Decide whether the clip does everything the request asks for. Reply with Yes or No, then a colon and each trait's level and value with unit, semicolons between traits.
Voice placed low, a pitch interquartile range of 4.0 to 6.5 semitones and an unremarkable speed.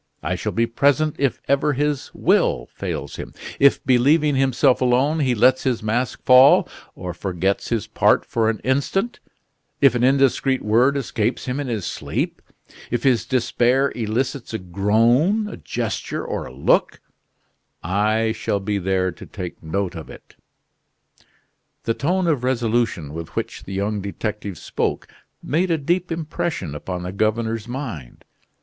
Yes: low, 120 Hz; average, 5.1 semitones; average, 155 wpm